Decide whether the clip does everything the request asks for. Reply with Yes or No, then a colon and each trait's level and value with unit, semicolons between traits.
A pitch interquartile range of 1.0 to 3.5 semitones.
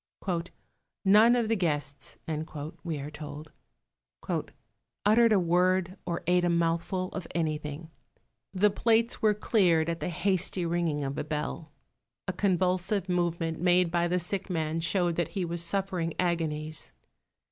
Yes: narrow, 2.6 semitones